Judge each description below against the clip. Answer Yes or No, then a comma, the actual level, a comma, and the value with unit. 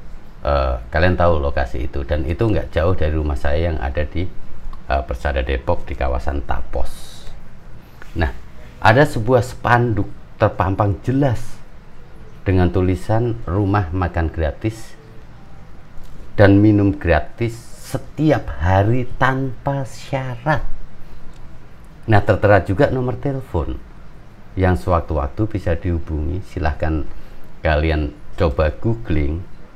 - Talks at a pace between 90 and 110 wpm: Yes, average, 105 wpm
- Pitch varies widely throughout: Yes, wide, 6.6 semitones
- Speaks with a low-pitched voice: Yes, very low, 95 Hz